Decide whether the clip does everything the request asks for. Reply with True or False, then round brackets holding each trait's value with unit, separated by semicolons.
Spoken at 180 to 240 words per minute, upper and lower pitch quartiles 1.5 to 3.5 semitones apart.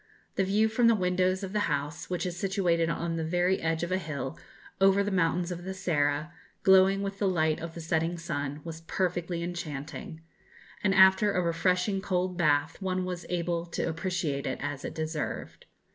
True (190 wpm; 2.7 semitones)